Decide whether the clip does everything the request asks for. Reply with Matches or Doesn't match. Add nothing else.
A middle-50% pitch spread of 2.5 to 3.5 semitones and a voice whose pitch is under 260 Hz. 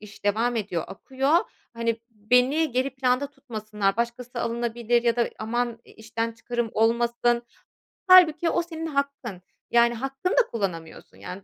Matches